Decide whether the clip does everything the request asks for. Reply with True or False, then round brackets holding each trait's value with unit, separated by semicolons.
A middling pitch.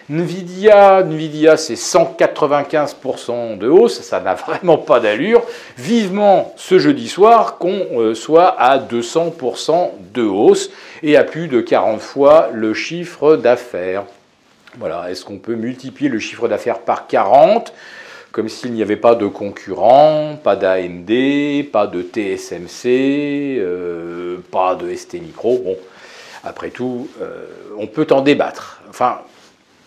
True (145 Hz)